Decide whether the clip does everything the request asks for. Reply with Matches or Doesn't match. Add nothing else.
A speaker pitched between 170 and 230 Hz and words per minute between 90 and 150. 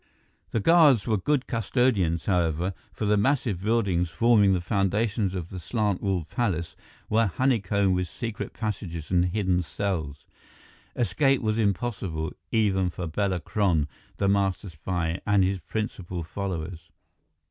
Doesn't match